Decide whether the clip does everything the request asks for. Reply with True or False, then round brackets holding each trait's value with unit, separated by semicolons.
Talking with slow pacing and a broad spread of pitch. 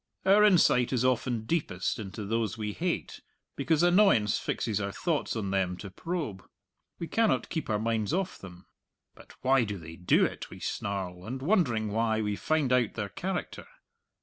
False (170 wpm; 7.7 semitones)